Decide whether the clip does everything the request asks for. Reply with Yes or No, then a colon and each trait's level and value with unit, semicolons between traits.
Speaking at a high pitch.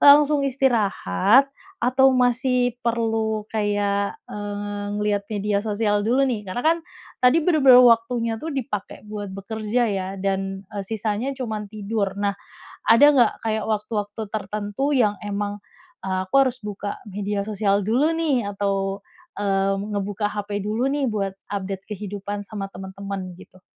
Yes: high, 210 Hz